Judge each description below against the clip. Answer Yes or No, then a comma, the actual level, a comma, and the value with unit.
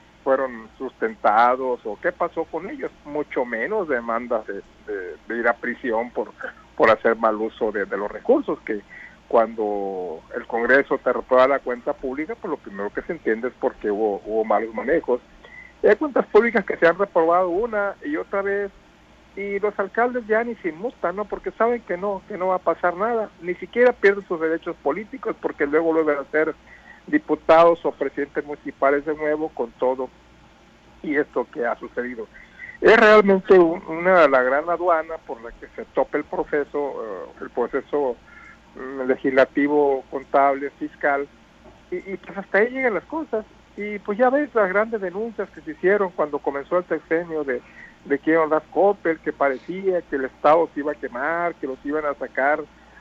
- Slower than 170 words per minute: No, average, 185 wpm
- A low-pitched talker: No, medium, 170 Hz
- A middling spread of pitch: No, wide, 6.3 semitones